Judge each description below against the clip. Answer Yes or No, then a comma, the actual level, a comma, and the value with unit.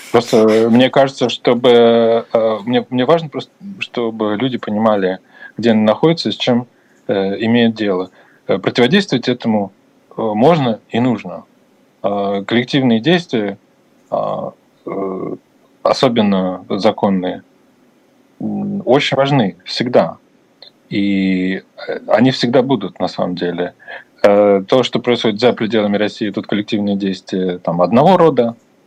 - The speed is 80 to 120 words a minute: Yes, slow, 110 wpm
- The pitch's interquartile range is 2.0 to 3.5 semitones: No, average, 3.9 semitones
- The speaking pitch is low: Yes, low, 115 Hz